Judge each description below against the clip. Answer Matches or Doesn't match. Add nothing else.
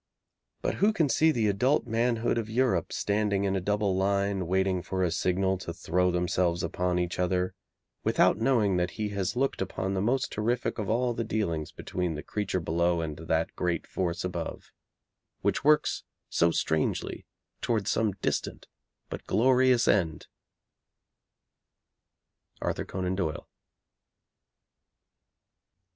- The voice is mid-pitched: Doesn't match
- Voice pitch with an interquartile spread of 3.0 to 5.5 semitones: Matches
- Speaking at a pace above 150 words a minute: Doesn't match